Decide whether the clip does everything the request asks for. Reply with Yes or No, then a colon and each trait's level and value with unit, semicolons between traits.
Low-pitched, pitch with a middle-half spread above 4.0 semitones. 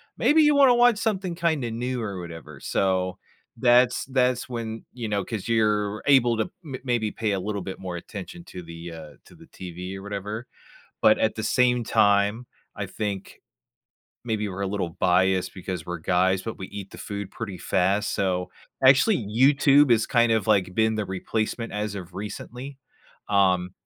Yes: low, 105 Hz; average, 4.5 semitones